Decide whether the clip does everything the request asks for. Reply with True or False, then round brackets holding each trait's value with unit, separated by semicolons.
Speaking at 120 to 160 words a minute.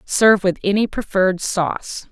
True (140 wpm)